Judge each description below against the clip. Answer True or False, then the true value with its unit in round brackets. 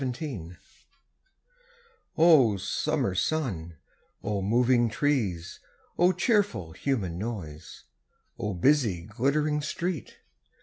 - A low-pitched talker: True (120 Hz)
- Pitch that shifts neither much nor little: False (8.0 semitones)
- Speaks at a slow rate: True (80 wpm)